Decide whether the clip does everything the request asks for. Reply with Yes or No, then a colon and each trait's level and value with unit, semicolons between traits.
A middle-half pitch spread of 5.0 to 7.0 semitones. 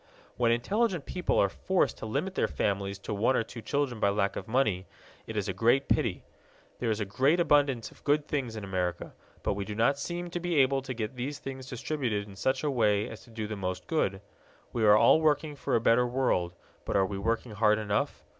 Yes: average, 5.3 semitones